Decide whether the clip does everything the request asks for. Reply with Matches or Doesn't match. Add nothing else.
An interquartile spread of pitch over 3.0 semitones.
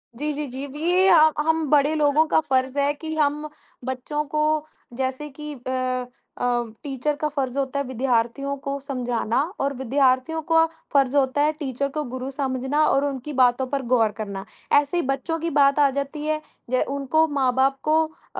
Doesn't match